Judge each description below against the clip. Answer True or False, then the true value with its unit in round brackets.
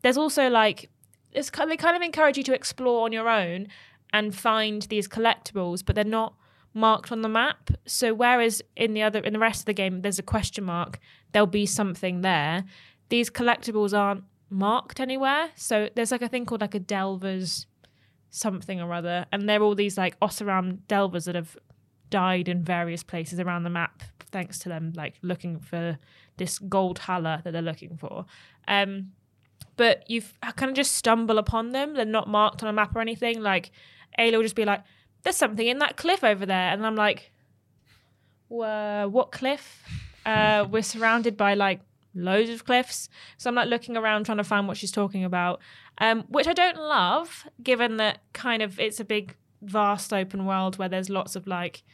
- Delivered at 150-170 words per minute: False (195 wpm)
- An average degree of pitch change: True (4.1 semitones)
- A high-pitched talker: True (205 Hz)